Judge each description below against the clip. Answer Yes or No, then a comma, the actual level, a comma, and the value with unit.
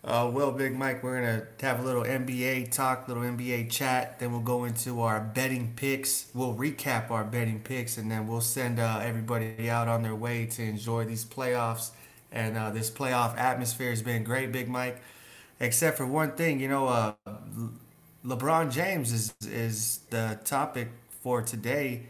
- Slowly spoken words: No, average, 180 wpm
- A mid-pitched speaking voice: No, low, 120 Hz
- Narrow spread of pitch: Yes, narrow, 2.3 semitones